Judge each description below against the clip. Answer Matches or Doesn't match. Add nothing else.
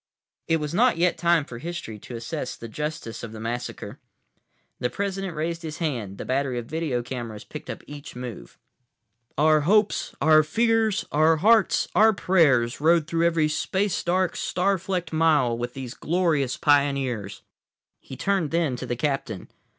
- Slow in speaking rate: Doesn't match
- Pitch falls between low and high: Matches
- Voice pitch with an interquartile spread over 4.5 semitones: Matches